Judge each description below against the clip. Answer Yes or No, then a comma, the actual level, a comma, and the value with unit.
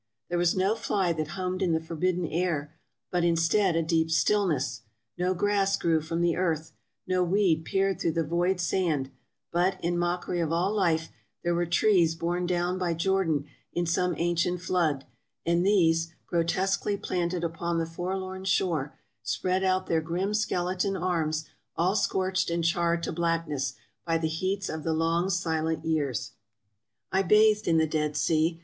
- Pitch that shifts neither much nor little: No, narrow, 2.2 semitones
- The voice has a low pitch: No, medium, 170 Hz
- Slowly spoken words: No, average, 170 wpm